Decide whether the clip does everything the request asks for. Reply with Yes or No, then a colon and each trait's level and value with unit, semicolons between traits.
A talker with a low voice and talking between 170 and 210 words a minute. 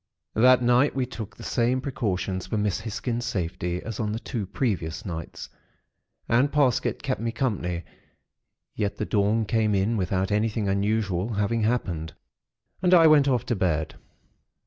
No: low, 110 Hz; average, 155 wpm